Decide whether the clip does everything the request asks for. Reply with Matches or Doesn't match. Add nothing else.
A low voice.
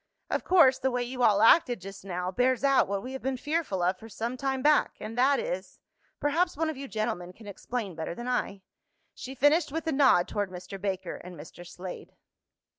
Doesn't match